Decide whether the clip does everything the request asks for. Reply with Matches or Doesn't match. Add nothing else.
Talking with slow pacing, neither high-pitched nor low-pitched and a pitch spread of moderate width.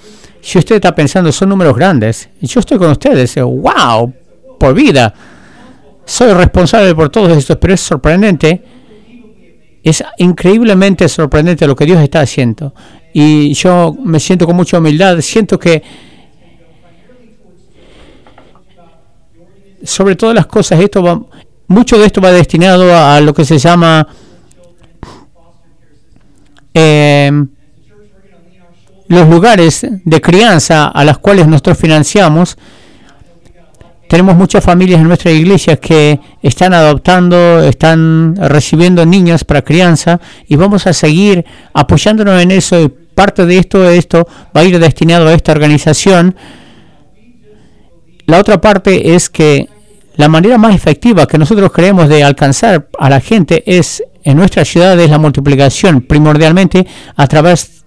Matches